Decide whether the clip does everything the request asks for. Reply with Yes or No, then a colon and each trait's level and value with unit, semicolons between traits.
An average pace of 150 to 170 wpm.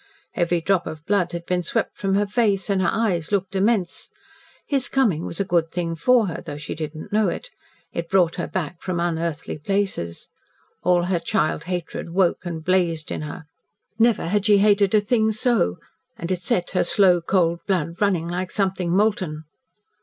No: average, 190 wpm